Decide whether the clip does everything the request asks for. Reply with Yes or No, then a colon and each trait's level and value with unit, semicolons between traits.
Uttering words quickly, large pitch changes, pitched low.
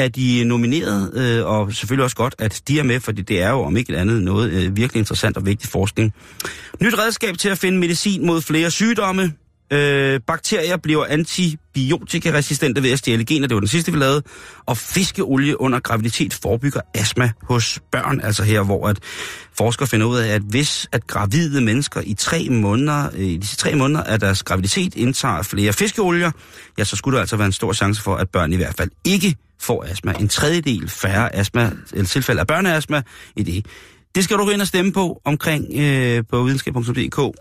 No: average, 195 wpm; wide, 6.5 semitones; low, 125 Hz